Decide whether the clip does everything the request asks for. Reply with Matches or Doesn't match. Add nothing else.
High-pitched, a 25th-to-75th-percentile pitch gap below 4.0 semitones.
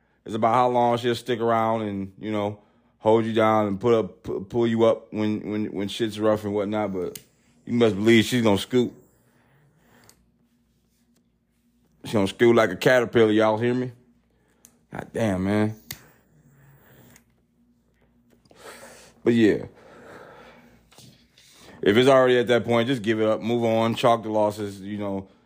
Doesn't match